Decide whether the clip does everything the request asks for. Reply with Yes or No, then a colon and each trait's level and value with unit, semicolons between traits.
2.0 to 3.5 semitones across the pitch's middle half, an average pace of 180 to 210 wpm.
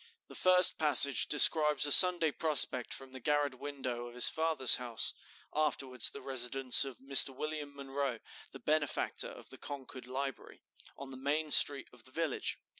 No: narrow, 2.6 semitones; average, 165 wpm